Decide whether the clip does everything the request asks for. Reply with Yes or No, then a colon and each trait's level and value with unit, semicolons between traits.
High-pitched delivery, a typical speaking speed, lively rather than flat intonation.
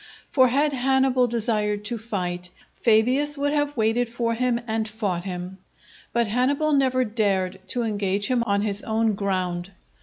No: high, 225 Hz; average, 155 wpm; average, 4.0 semitones